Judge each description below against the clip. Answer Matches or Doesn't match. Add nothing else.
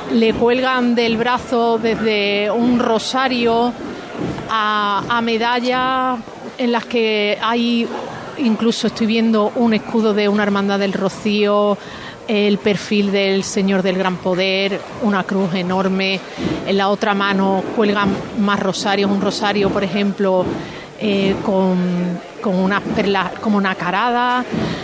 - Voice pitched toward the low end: Doesn't match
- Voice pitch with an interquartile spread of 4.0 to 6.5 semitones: Doesn't match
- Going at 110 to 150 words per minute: Matches